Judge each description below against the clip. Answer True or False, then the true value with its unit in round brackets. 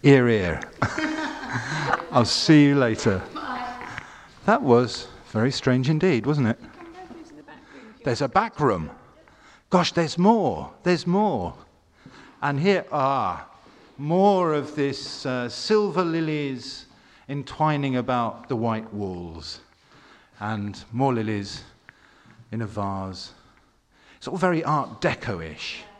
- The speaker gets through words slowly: True (115 wpm)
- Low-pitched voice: True (130 Hz)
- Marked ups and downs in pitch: True (7.6 semitones)